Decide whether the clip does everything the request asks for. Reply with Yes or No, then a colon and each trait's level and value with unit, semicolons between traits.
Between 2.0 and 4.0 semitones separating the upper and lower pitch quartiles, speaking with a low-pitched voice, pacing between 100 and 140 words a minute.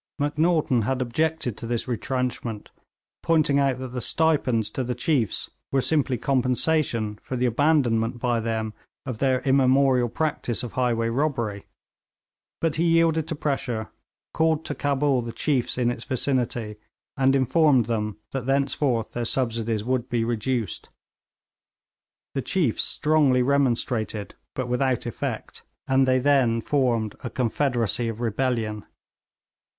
Yes: average, 3.3 semitones; low, 125 Hz; slow, 135 wpm